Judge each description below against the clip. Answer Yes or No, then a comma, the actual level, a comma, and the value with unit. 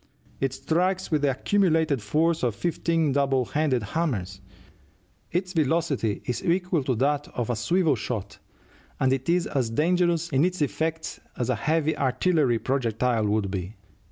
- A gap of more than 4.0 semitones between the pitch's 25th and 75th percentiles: Yes, wide, 5.4 semitones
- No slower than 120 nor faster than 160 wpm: Yes, average, 155 wpm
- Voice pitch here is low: No, medium, 145 Hz